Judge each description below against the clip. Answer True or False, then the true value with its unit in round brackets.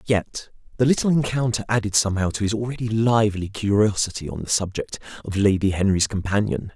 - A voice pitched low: True (105 Hz)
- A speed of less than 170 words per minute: True (160 wpm)